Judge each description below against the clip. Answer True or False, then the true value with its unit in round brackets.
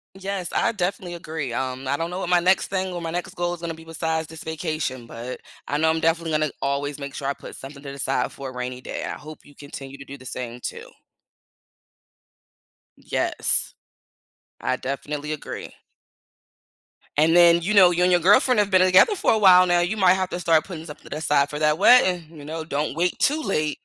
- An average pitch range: True (4.0 semitones)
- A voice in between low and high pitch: True (160 Hz)